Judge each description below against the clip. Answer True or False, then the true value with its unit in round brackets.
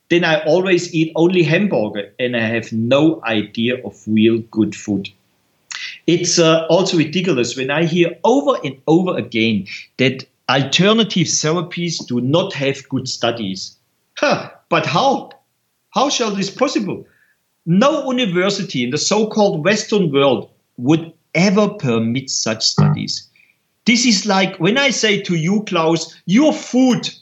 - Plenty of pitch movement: True (7.8 semitones)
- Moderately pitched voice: True (160 Hz)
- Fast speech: False (140 wpm)